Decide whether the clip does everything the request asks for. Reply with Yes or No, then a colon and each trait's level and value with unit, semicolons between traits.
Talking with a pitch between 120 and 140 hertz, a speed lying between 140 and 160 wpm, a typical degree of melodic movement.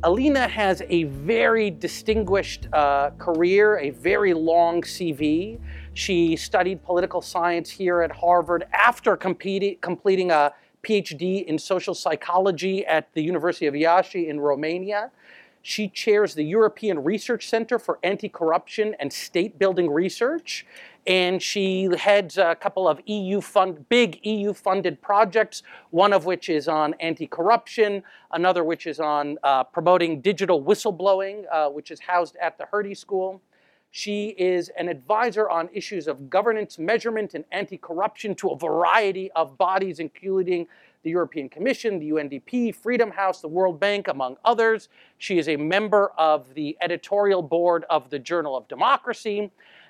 No: medium, 185 Hz; average, 145 wpm; average, 3.8 semitones